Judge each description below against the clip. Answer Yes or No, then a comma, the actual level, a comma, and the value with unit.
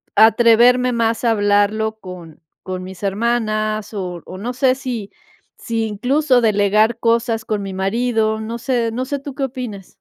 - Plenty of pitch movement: No, average, 3.0 semitones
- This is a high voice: Yes, high, 225 Hz